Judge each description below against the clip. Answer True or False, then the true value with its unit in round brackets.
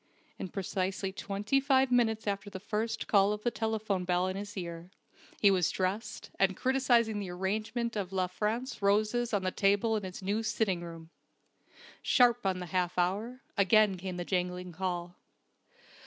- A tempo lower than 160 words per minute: False (170 wpm)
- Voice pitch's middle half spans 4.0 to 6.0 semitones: False (3.2 semitones)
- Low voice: False (200 Hz)